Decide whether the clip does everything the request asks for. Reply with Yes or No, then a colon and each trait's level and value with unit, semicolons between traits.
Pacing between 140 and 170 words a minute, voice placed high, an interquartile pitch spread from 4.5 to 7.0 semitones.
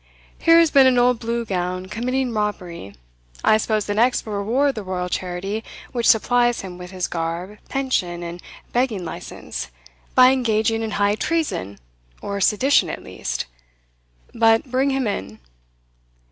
Yes: average, 150 wpm; high, 215 Hz; average, 5.3 semitones